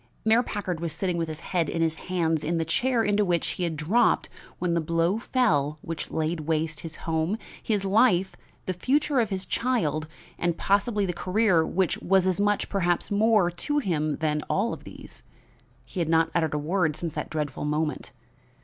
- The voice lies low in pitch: No, medium, 175 Hz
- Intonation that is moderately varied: Yes, average, 4.1 semitones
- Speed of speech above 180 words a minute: Yes, average, 190 wpm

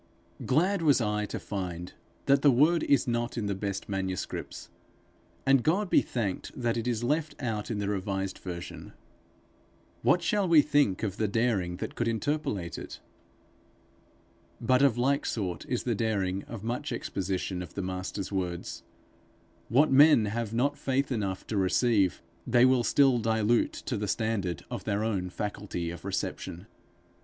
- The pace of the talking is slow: No, average, 160 wpm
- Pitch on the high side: No, low, 110 Hz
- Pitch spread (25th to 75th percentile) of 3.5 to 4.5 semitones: No, average, 5.0 semitones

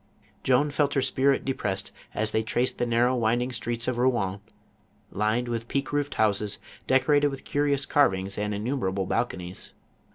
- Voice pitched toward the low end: Yes, low, 120 Hz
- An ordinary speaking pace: Yes, average, 160 wpm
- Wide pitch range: No, average, 4.2 semitones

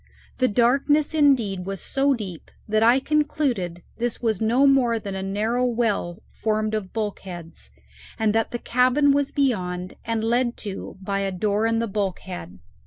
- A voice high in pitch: Yes, high, 225 Hz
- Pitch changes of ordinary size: Yes, average, 4.4 semitones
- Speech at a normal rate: Yes, average, 165 wpm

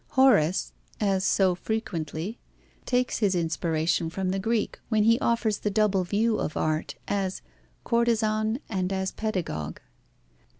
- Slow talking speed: Yes, slow, 130 wpm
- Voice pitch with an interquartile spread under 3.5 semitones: No, average, 3.8 semitones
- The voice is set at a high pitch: Yes, high, 200 Hz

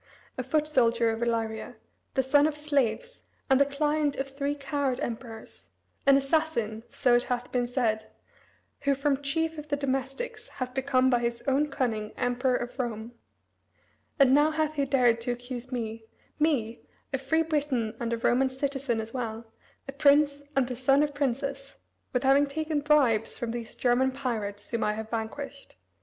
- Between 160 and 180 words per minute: Yes, average, 175 wpm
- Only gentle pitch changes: No, average, 3.2 semitones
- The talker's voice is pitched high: Yes, very high, 265 Hz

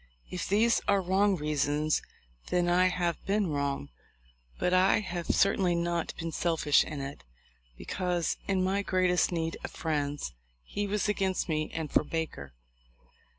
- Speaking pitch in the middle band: Yes, medium, 175 Hz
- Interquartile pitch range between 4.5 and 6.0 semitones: No, average, 3.5 semitones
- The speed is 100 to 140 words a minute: No, average, 150 wpm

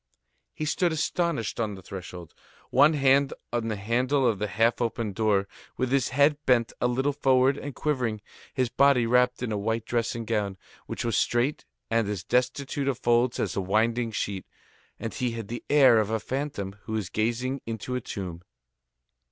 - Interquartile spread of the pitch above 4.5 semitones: No, average, 3.6 semitones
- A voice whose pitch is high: No, low, 120 Hz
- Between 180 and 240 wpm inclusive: Yes, average, 185 wpm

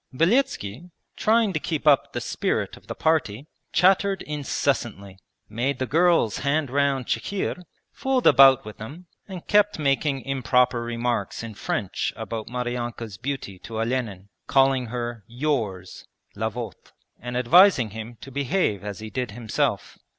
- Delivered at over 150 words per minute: No, average, 145 wpm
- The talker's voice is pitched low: Yes, low, 125 Hz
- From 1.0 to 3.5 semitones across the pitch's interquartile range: No, average, 4.9 semitones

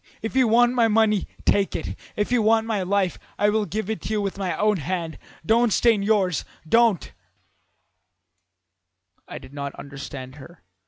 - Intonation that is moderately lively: No, wide, 7.2 semitones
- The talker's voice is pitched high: Yes, high, 200 Hz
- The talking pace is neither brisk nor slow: Yes, average, 175 wpm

